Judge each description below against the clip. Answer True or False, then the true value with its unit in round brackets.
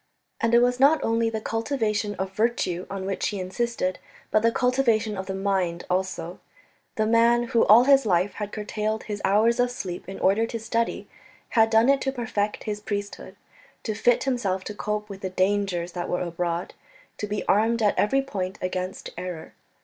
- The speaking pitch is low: False (210 Hz)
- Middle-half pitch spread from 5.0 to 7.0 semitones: False (3.4 semitones)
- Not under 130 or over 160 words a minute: False (190 wpm)